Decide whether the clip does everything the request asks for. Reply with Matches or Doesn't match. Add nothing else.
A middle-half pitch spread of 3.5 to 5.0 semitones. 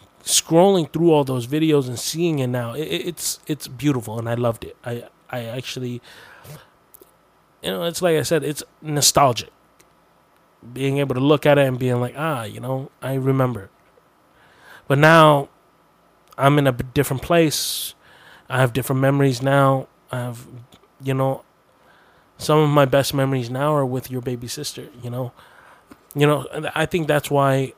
Doesn't match